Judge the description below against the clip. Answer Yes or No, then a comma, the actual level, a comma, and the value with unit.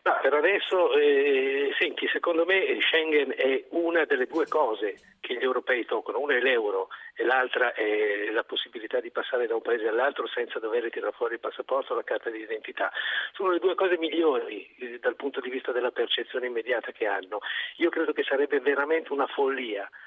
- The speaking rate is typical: No, fast, 190 wpm